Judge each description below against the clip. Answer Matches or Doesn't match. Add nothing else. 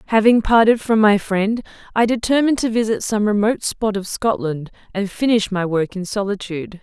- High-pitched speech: Matches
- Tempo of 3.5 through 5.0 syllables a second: Doesn't match